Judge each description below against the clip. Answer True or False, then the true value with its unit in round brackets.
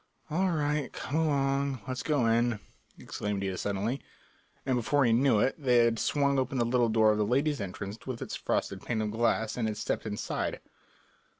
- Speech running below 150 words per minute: False (190 wpm)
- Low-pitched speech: True (120 Hz)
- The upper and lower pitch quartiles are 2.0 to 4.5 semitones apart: True (4.1 semitones)